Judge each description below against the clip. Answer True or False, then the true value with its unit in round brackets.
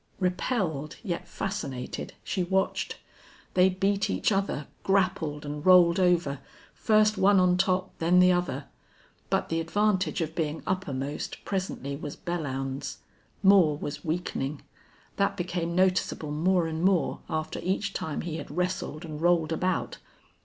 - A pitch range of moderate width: True (3.5 semitones)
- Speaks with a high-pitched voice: False (175 Hz)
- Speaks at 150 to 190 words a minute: False (140 wpm)